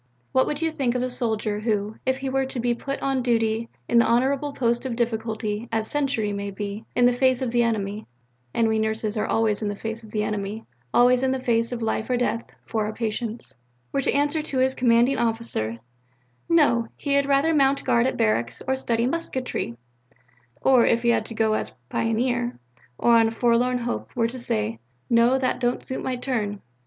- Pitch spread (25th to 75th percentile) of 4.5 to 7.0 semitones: No, average, 2.8 semitones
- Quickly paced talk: Yes, fast, 210 wpm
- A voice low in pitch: No, high, 235 Hz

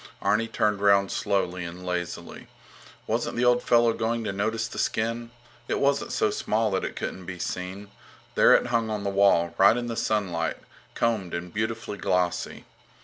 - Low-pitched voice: Yes, low, 105 Hz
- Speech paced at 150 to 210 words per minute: Yes, average, 175 wpm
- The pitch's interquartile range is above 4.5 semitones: No, average, 3.7 semitones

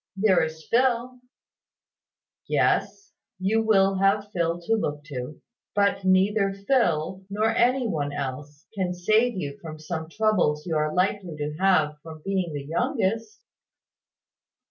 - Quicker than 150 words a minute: No, average, 140 wpm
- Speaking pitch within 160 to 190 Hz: Yes, medium, 185 Hz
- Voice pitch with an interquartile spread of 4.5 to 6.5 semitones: Yes, wide, 5.5 semitones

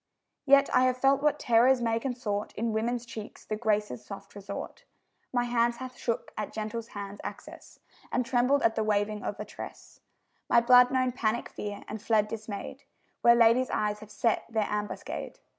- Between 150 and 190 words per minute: Yes, average, 175 wpm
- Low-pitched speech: No, high, 230 Hz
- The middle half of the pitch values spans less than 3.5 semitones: Yes, average, 2.8 semitones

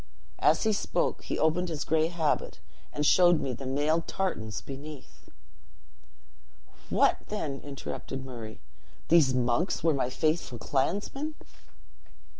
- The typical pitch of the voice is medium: Yes, medium, 150 Hz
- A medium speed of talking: No, slow, 120 wpm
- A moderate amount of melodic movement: Yes, average, 4.3 semitones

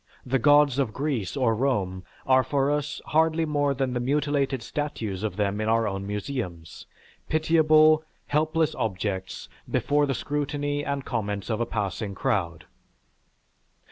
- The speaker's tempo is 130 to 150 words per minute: Yes, average, 140 wpm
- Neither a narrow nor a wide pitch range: No, wide, 6.0 semitones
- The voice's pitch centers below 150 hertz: Yes, low, 135 Hz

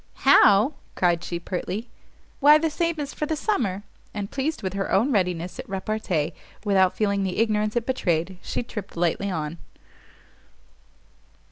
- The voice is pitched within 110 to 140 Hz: No, high, 200 Hz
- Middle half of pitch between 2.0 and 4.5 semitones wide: No, wide, 5.4 semitones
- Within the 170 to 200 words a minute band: No, average, 150 wpm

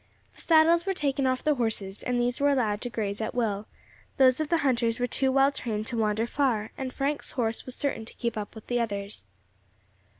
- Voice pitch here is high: Yes, high, 245 Hz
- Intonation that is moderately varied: Yes, average, 3.7 semitones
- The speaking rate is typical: No, fast, 210 wpm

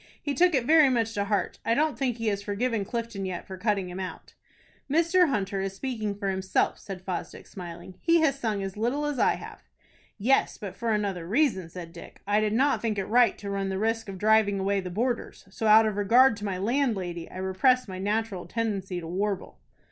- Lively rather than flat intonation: No, average, 3.8 semitones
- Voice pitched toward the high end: Yes, high, 210 Hz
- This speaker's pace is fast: Yes, fast, 215 wpm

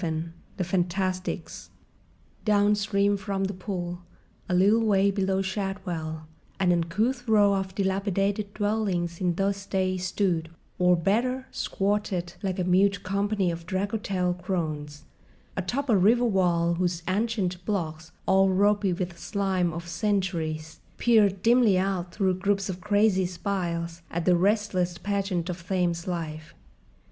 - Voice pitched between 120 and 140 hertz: No, high, 190 Hz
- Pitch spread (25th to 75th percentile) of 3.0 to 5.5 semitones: No, narrow, 2.5 semitones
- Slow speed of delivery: Yes, slow, 130 wpm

